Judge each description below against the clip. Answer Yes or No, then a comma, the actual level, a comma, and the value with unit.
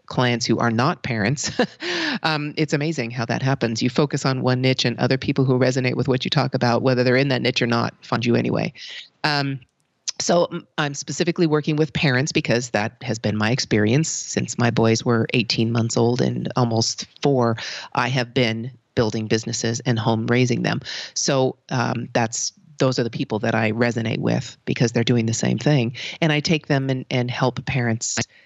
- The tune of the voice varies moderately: Yes, average, 3.5 semitones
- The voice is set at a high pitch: No, low, 125 Hz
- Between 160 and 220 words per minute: Yes, average, 195 wpm